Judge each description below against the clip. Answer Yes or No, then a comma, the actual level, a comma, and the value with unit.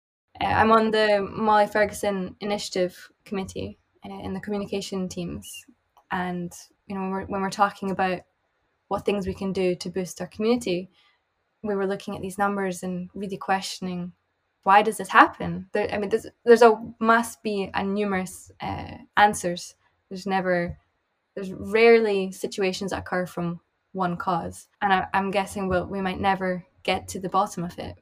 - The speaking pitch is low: No, high, 195 Hz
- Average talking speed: Yes, average, 170 wpm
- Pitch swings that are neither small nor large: No, narrow, 1.9 semitones